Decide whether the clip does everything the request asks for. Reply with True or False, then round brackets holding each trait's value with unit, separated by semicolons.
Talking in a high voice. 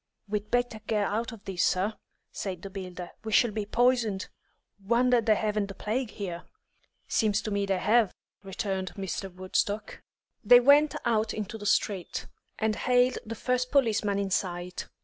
True (210 Hz)